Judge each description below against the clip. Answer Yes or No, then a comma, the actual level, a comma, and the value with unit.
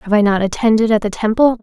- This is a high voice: Yes, high, 215 Hz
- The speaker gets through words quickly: Yes, fast, 260 wpm